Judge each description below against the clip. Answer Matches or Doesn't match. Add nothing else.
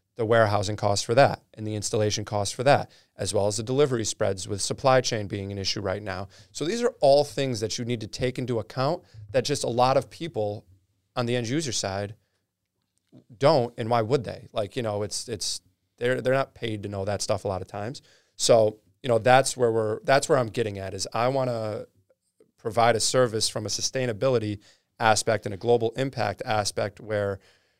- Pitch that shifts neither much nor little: Matches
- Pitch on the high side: Doesn't match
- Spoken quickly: Matches